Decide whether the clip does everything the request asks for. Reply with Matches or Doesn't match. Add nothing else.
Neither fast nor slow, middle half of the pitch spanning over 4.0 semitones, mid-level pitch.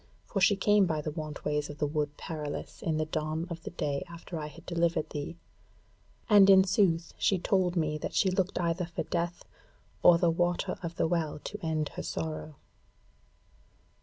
Doesn't match